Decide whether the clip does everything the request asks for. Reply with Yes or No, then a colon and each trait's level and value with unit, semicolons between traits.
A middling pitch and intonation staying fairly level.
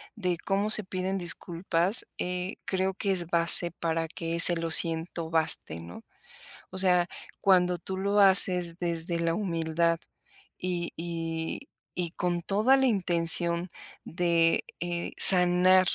Yes: medium, 175 Hz; narrow, 2.0 semitones